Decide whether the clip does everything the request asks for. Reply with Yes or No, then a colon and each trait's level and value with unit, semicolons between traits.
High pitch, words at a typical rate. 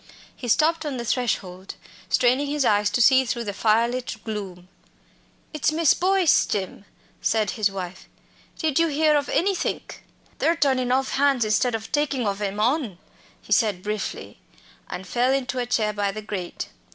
Yes: high, 240 Hz; average, 170 wpm